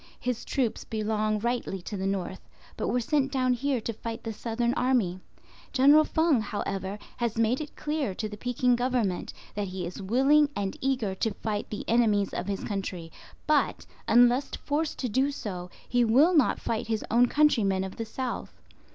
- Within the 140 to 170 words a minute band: No, average, 180 wpm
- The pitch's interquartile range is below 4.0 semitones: No, average, 4.3 semitones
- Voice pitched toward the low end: No, high, 230 Hz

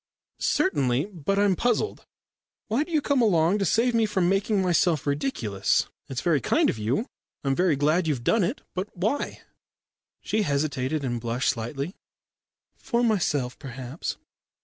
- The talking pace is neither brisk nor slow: Yes, average, 150 wpm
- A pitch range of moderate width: No, wide, 7.6 semitones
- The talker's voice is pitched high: No, medium, 170 Hz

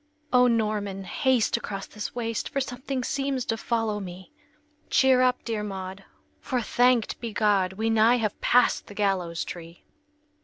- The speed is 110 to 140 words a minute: No, average, 155 wpm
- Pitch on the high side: Yes, high, 220 Hz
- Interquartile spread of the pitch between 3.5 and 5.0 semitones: Yes, average, 4.1 semitones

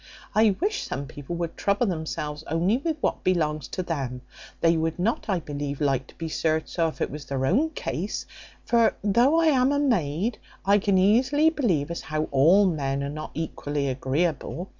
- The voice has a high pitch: No, medium, 170 Hz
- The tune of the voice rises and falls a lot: Yes, wide, 6.6 semitones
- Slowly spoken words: No, average, 190 wpm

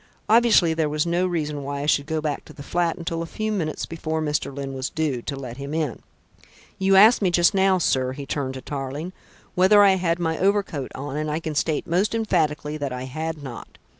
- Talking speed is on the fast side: Yes, fast, 225 wpm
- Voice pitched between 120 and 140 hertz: No, medium, 155 Hz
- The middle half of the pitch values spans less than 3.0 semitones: No, average, 3.8 semitones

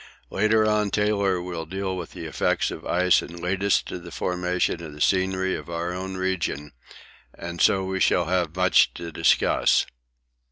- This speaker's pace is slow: No, average, 175 wpm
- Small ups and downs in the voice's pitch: Yes, narrow, 1.8 semitones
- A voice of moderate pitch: No, very low, 90 Hz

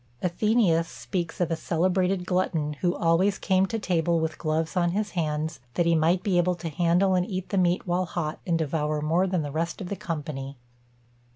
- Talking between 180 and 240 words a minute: Yes, average, 200 wpm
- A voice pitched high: No, medium, 175 Hz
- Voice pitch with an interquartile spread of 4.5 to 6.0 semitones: No, narrow, 2.5 semitones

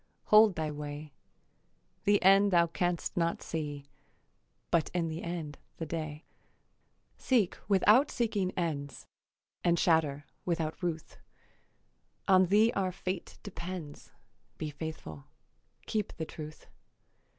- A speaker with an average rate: No, slow, 115 wpm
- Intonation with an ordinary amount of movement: Yes, average, 3.4 semitones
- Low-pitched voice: No, medium, 170 Hz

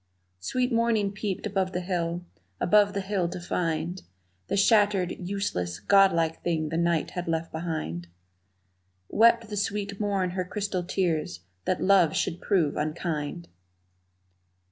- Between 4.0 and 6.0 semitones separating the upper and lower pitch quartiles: No, average, 3.3 semitones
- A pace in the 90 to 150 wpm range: Yes, slow, 135 wpm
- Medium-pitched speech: Yes, medium, 180 Hz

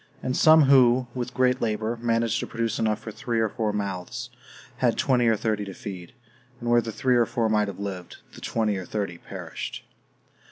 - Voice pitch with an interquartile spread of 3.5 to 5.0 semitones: No, narrow, 2.6 semitones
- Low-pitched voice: Yes, low, 115 Hz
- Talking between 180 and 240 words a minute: Yes, average, 200 wpm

